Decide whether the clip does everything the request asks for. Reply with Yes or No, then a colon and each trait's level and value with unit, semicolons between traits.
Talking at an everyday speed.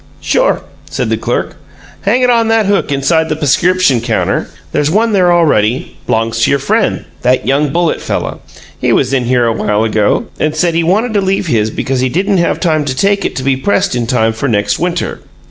No: fast, 210 wpm